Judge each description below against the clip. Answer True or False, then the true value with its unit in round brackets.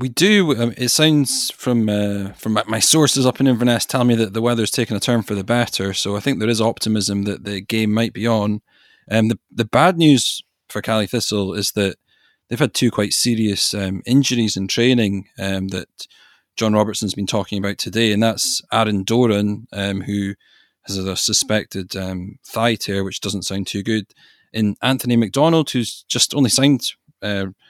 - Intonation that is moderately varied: True (3.3 semitones)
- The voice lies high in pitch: False (110 Hz)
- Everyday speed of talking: True (190 wpm)